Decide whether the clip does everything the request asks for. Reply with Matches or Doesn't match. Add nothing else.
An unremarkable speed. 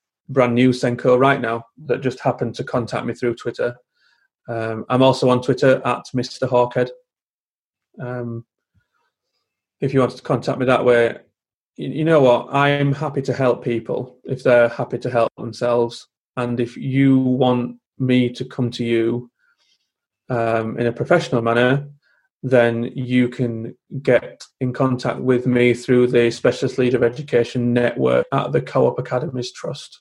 Matches